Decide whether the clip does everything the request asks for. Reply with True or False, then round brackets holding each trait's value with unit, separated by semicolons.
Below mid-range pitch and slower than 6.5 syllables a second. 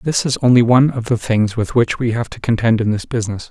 True (120 Hz; 6.3 syllables/s)